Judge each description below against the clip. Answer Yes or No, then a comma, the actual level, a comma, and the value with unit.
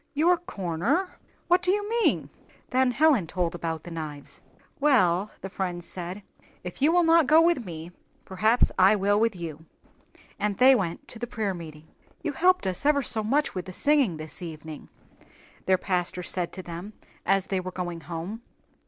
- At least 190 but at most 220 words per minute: No, average, 180 wpm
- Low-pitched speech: No, high, 195 Hz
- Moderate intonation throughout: No, wide, 8.0 semitones